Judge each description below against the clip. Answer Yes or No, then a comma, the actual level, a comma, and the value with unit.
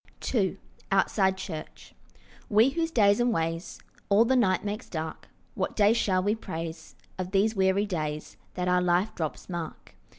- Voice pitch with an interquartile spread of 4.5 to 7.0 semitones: No, average, 3.5 semitones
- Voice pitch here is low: No, high, 190 Hz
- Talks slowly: No, average, 160 wpm